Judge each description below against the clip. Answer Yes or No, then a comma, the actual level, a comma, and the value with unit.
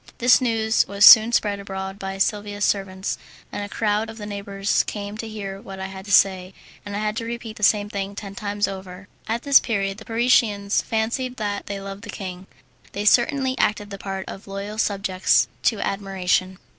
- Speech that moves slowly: No, average, 195 wpm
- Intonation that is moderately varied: No, narrow, 2.0 semitones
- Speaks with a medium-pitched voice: No, high, 205 Hz